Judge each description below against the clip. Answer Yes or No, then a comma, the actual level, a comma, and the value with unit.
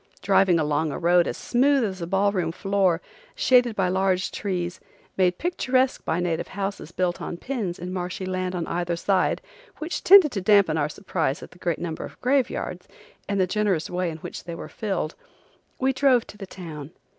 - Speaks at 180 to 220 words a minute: Yes, average, 190 wpm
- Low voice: No, medium, 185 Hz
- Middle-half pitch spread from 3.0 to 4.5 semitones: Yes, average, 3.4 semitones